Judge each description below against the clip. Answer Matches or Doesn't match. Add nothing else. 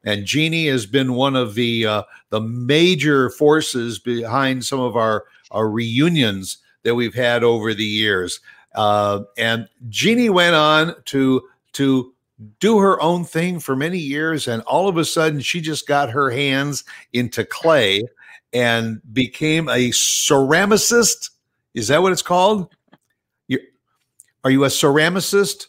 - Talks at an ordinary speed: Matches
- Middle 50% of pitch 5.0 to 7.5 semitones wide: Matches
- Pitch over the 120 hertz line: Matches